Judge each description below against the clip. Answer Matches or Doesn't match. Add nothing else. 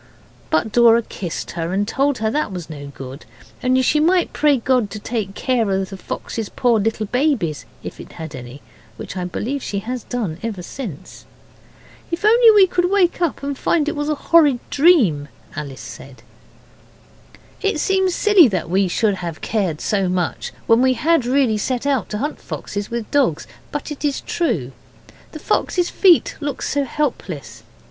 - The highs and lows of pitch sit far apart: Matches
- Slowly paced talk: Doesn't match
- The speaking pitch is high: Matches